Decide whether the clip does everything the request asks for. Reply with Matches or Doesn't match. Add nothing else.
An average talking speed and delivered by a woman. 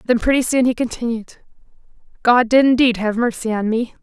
Matches